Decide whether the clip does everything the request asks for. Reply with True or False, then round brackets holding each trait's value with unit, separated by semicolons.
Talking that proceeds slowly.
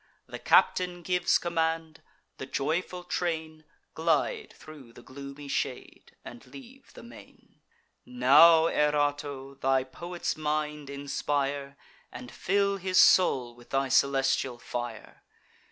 True (115 wpm)